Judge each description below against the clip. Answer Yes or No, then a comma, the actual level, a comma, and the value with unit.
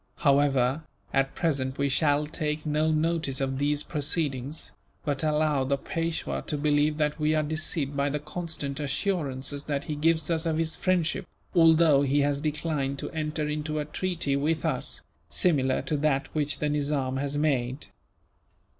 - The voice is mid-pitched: Yes, medium, 150 Hz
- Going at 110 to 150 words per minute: No, average, 165 wpm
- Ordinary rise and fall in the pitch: No, narrow, 2.0 semitones